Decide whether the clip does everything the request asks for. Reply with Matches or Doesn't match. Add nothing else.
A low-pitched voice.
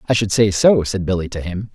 Matches